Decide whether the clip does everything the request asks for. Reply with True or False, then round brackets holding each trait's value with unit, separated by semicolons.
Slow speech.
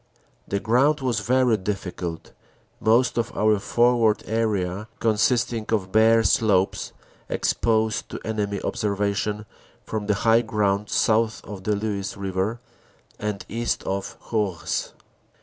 True (120 wpm)